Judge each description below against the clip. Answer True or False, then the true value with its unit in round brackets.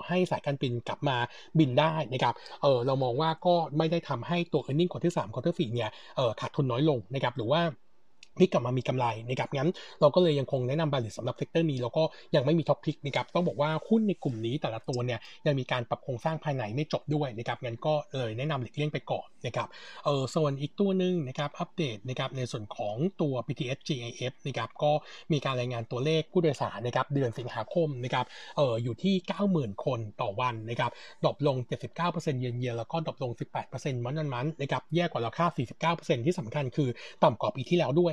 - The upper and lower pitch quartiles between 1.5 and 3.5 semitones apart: False (4.3 semitones)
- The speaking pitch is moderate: True (145 Hz)